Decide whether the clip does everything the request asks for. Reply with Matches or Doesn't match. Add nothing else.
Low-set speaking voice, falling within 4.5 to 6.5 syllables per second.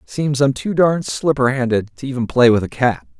Matches